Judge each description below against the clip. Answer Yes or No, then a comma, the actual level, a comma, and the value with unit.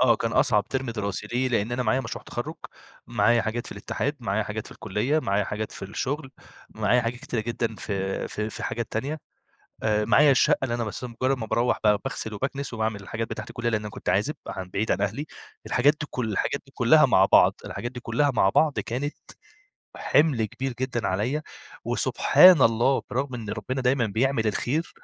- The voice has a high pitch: No, low, 120 Hz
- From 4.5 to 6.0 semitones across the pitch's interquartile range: No, average, 3.5 semitones